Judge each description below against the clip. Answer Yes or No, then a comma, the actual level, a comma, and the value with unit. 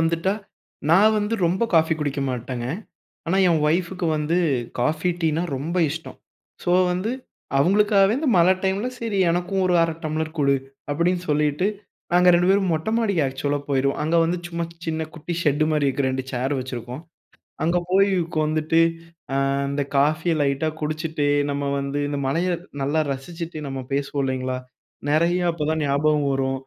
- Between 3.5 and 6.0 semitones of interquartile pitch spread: Yes, average, 3.8 semitones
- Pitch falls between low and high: Yes, medium, 160 Hz